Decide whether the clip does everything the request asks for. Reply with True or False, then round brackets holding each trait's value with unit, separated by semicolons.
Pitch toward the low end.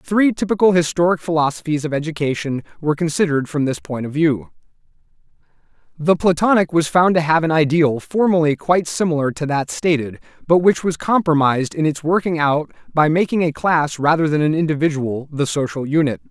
False (160 Hz)